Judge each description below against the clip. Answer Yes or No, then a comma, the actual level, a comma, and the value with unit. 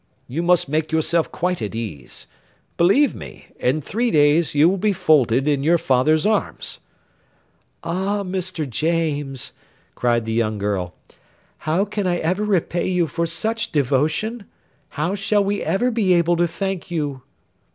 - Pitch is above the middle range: No, medium, 165 Hz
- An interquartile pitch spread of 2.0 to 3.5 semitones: No, average, 4.9 semitones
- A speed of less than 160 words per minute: Yes, average, 150 wpm